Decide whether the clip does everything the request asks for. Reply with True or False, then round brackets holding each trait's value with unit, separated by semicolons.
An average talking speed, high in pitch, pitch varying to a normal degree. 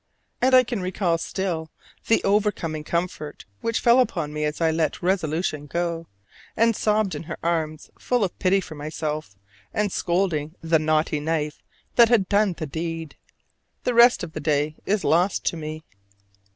False (165 wpm; 170 Hz; 4.2 semitones)